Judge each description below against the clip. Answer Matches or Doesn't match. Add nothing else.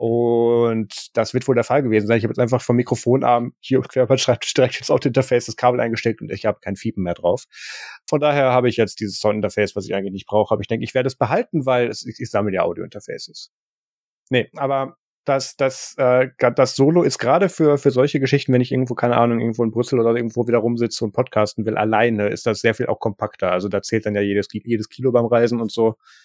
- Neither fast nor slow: Doesn't match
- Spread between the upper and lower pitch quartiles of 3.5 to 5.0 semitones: Doesn't match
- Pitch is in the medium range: Doesn't match